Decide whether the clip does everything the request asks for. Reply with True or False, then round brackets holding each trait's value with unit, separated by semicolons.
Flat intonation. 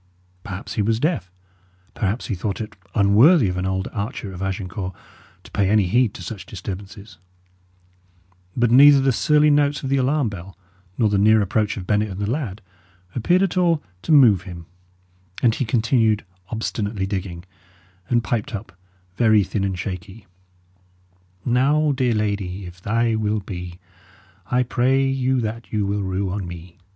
False (4.4 semitones)